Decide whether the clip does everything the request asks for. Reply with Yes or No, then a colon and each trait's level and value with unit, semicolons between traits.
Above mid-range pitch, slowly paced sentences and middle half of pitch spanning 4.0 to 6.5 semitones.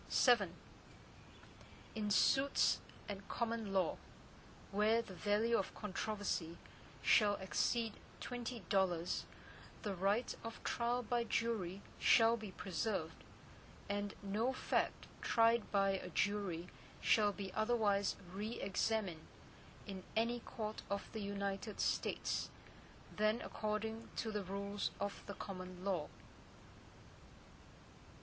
No: high, 205 Hz; slow, 110 wpm; narrow, 2.5 semitones